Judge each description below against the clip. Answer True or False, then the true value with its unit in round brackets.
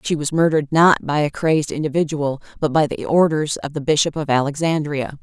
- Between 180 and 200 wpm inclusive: True (195 wpm)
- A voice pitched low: False (150 Hz)